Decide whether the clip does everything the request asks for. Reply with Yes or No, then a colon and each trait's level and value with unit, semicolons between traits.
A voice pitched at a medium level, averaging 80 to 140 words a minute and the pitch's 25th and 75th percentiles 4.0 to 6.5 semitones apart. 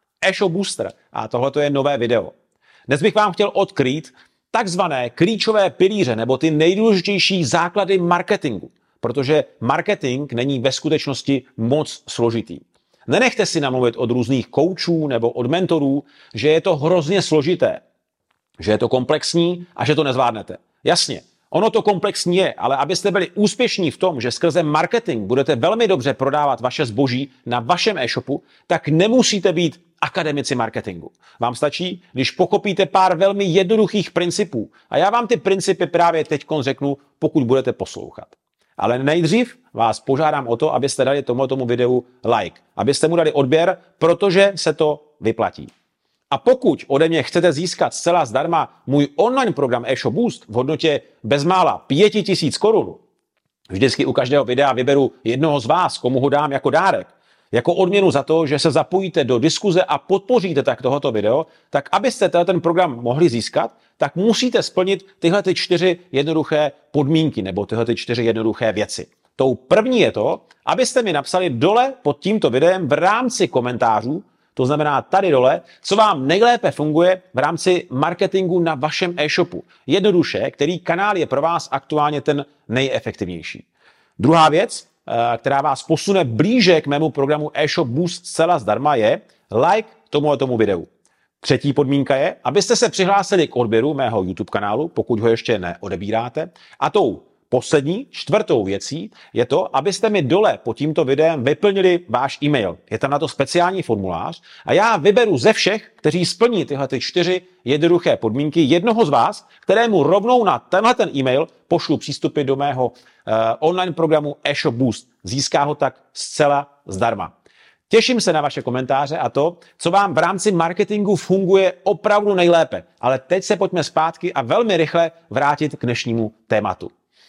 No: medium, 155 Hz; average, 155 wpm; average, 5.3 semitones